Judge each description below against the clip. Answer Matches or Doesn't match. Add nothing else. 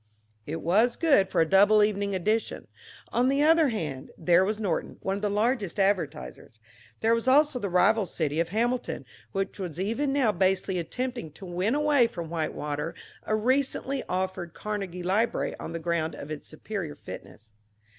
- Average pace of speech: Matches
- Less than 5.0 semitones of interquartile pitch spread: Doesn't match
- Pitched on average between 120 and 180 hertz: Doesn't match